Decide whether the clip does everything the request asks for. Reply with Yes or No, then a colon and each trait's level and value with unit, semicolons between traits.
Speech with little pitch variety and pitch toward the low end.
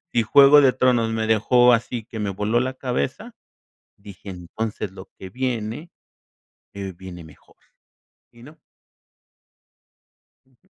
No: average, 4.0 semitones; low, 115 Hz